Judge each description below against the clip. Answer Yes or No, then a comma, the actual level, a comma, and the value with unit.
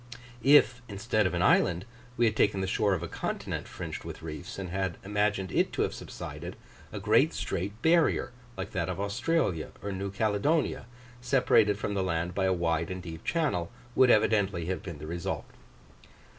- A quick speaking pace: No, average, 185 wpm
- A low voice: Yes, very low, 95 Hz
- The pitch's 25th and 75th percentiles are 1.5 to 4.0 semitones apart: Yes, average, 3.4 semitones